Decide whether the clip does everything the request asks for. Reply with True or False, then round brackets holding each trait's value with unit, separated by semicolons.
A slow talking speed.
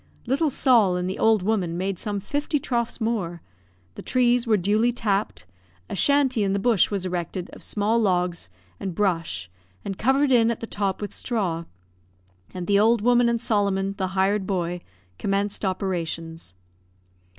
False (160 wpm)